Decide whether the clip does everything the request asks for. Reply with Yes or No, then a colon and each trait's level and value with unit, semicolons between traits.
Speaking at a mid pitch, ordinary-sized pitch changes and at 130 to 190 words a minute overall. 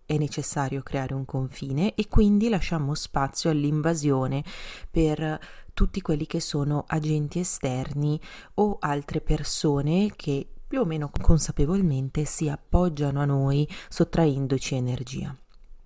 No: medium, 150 Hz; average, 3.1 semitones; slow, 115 wpm